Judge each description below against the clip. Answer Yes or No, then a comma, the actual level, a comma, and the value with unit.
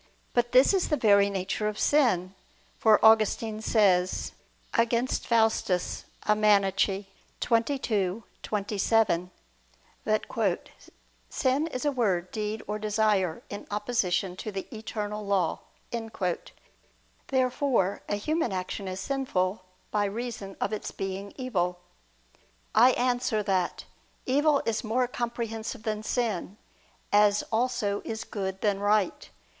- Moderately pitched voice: No, high, 215 Hz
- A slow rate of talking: Yes, slow, 115 wpm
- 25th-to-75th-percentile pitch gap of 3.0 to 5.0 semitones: Yes, average, 3.3 semitones